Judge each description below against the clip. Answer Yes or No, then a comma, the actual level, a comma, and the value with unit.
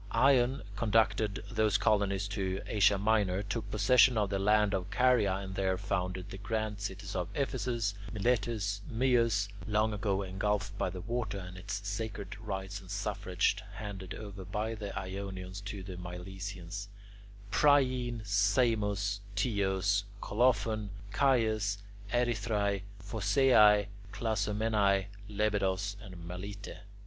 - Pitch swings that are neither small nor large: No, narrow, 2.2 semitones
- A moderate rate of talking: No, slow, 120 wpm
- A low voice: Yes, low, 100 Hz